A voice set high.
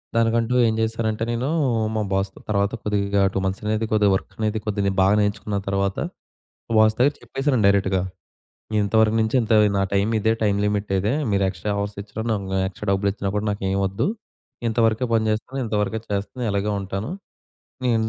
No: low, 105 Hz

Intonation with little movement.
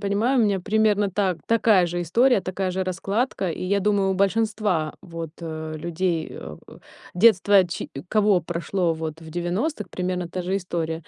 No: average, 3.2 semitones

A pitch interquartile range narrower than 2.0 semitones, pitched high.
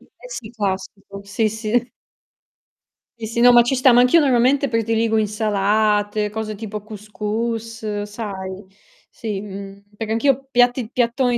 No: narrow, 2.5 semitones; high, 220 Hz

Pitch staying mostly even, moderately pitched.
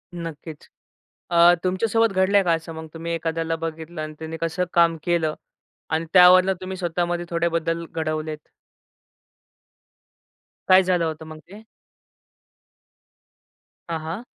Yes: narrow, 2.0 semitones; medium, 170 Hz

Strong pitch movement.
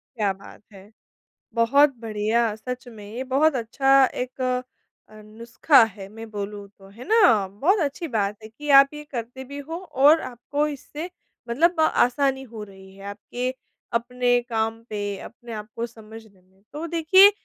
No: average, 4.6 semitones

